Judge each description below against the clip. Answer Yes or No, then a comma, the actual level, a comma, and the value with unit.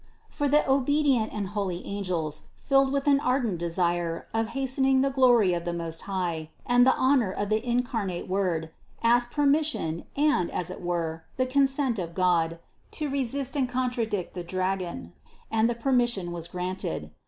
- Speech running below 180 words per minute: Yes, average, 165 wpm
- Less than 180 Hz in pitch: No, high, 215 Hz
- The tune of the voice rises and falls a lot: Yes, wide, 7.1 semitones